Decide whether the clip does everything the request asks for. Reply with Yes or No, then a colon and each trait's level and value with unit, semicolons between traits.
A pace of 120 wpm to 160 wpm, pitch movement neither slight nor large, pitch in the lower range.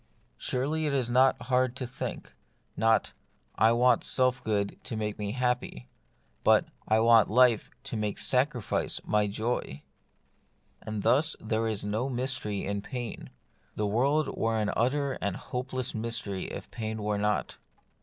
Yes: average, 155 wpm; average, 3.3 semitones; low, 115 Hz